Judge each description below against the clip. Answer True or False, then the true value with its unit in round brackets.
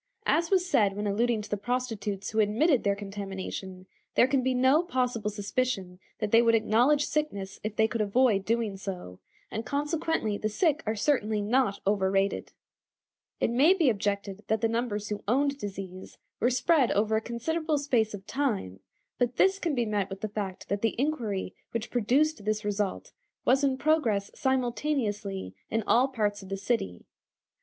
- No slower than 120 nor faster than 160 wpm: False (175 wpm)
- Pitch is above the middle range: True (220 Hz)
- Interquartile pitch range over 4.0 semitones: True (4.4 semitones)